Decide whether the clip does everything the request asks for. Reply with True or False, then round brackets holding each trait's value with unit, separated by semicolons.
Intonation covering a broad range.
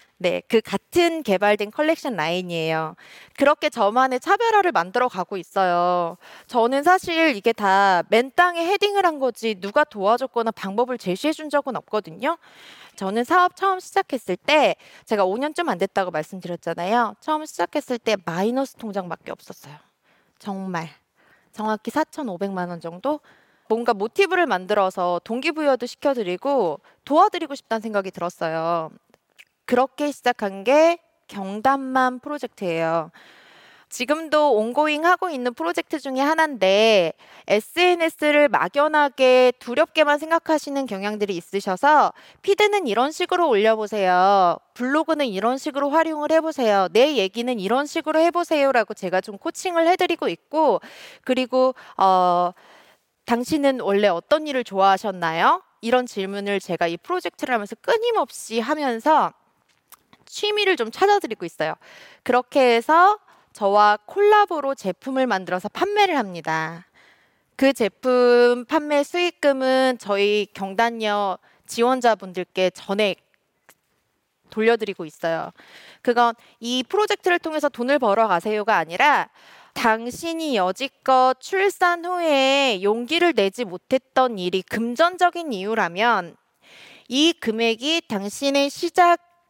True (7.4 semitones)